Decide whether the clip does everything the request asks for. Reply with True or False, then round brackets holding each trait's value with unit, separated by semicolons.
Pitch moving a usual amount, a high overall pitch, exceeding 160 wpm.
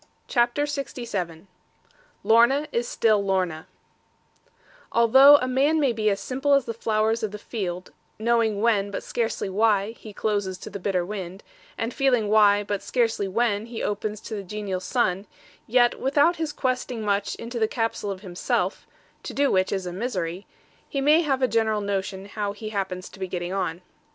True (3.6 semitones; 215 Hz; 175 wpm)